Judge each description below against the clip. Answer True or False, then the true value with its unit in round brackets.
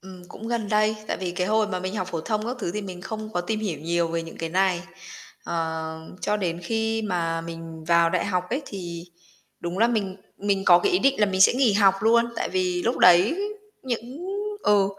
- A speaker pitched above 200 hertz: False (190 Hz)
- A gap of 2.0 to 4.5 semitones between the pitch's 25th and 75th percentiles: True (4.0 semitones)